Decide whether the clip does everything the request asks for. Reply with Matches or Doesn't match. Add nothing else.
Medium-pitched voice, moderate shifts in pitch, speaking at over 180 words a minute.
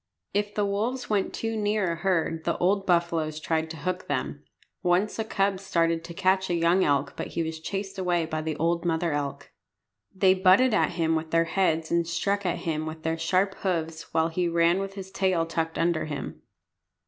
Matches